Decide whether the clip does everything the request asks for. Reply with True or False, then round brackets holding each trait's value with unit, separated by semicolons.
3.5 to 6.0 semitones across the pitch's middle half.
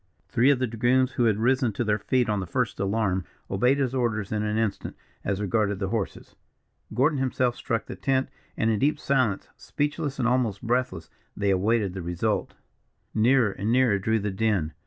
True (4.1 semitones)